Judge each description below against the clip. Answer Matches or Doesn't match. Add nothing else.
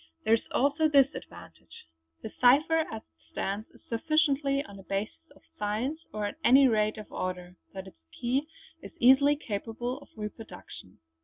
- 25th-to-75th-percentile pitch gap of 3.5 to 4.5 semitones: Doesn't match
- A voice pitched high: Matches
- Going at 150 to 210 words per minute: Matches